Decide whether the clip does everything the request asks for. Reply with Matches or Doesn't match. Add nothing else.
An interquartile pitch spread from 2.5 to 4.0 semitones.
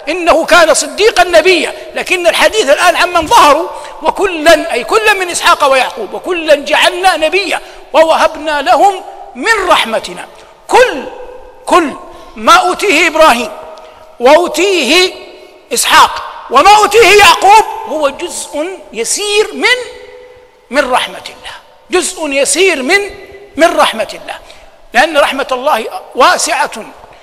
Doesn't match